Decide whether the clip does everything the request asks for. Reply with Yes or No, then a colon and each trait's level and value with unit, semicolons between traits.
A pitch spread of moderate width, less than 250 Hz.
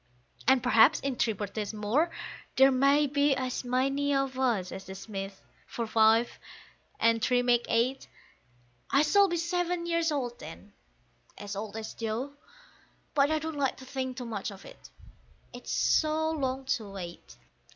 No: average, 4.4 semitones; very high, 255 Hz